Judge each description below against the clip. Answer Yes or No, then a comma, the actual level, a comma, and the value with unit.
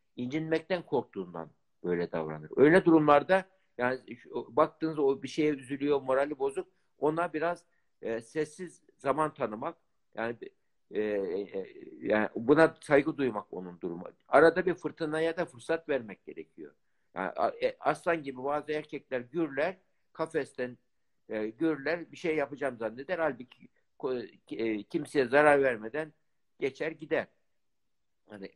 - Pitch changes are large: No, average, 4.5 semitones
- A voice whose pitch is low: No, medium, 150 Hz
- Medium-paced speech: Yes, average, 120 wpm